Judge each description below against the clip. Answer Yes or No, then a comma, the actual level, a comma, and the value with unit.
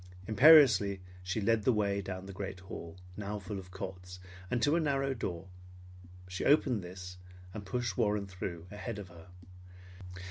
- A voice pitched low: Yes, low, 100 Hz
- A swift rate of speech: No, average, 165 wpm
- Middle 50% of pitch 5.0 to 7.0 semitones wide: No, average, 3.7 semitones